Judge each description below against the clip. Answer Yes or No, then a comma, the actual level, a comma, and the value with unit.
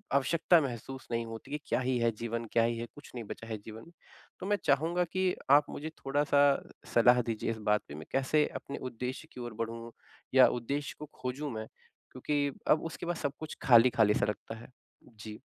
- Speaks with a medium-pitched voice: No, low, 125 Hz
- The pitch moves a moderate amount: Yes, average, 4.1 semitones